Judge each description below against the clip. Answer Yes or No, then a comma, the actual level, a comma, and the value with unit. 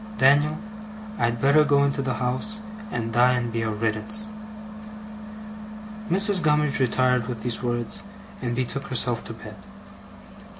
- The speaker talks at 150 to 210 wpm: No, slow, 135 wpm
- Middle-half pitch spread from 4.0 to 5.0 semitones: No, average, 3.5 semitones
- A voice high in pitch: No, low, 125 Hz